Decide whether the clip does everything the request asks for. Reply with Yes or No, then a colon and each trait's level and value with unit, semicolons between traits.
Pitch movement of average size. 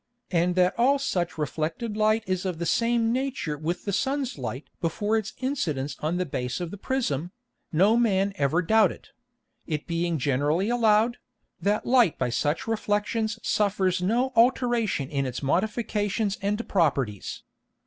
No: wide, 6.0 semitones